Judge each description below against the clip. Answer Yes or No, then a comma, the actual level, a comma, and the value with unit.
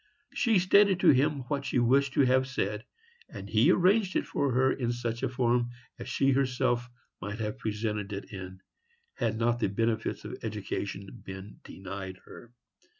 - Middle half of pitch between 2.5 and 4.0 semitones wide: No, average, 4.4 semitones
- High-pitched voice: No, low, 120 Hz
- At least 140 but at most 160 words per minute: No, average, 170 wpm